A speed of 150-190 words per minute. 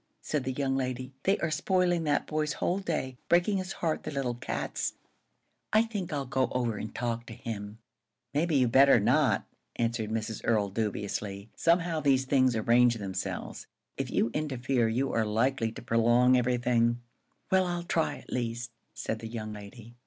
Yes: average, 175 wpm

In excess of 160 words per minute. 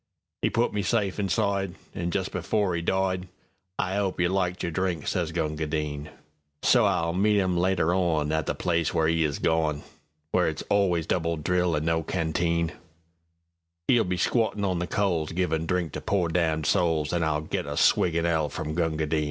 Yes: average, 170 wpm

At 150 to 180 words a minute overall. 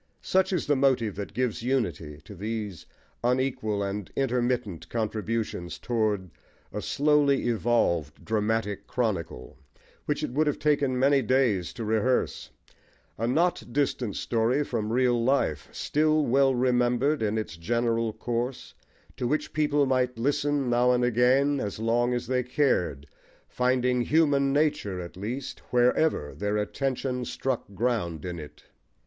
No: average, 140 wpm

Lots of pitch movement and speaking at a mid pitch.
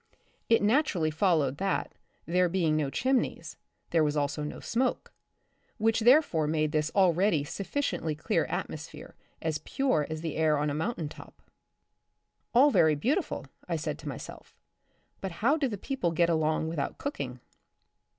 Yes: wide, 6.7 semitones; medium, 165 Hz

